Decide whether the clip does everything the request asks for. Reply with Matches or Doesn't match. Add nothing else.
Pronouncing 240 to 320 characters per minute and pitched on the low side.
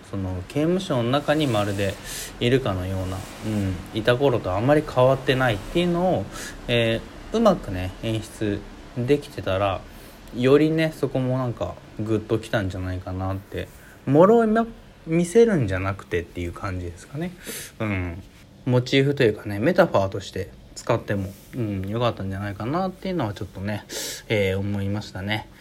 Matches